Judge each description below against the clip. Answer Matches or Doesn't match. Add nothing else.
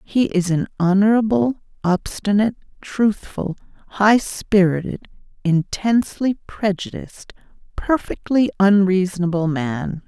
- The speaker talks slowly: Matches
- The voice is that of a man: Doesn't match